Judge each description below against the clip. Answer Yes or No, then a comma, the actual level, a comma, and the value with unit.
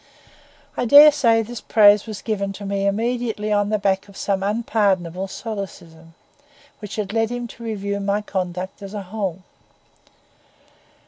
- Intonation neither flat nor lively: No, narrow, 2.3 semitones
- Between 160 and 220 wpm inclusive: No, average, 145 wpm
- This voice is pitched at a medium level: No, high, 205 Hz